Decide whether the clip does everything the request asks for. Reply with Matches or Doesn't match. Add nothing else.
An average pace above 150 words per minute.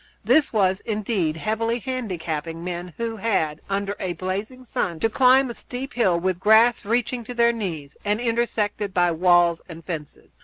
Matches